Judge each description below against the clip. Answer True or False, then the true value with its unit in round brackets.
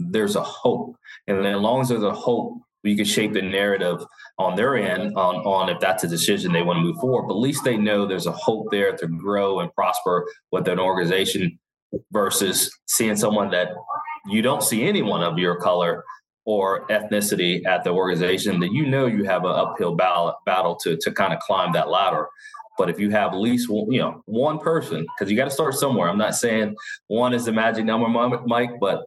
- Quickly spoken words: True (215 wpm)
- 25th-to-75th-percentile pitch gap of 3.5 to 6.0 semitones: True (4.5 semitones)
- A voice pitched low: True (105 Hz)